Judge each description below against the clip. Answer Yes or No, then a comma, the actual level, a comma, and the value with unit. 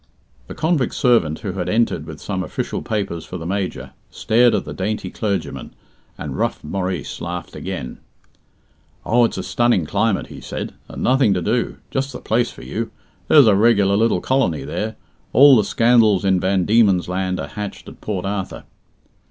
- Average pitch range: Yes, average, 4.2 semitones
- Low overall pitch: Yes, low, 100 Hz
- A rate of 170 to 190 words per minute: Yes, average, 175 wpm